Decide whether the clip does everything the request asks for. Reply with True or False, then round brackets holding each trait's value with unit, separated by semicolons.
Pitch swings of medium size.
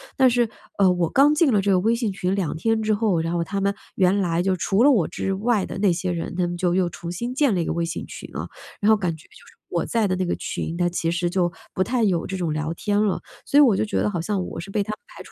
True (3.6 semitones)